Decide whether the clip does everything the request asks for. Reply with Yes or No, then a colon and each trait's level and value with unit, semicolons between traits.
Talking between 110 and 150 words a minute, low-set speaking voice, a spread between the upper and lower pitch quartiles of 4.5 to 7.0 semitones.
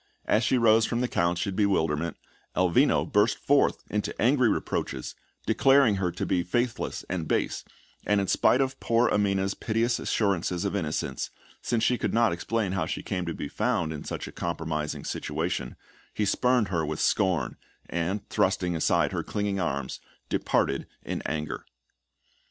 No: average, 165 wpm; low, 100 Hz; average, 5.1 semitones